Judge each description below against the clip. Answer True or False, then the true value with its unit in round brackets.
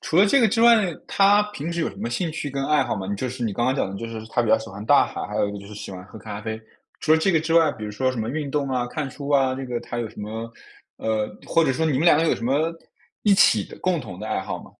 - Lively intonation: True (6.4 semitones)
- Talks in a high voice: False (130 Hz)